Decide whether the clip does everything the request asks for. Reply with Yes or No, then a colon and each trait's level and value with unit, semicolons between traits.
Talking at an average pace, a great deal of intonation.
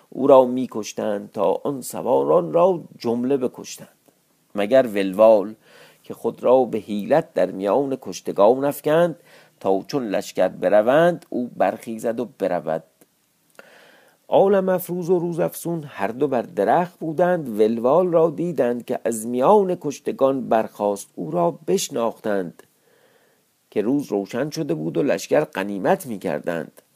Yes: average, 130 wpm; wide, 7.8 semitones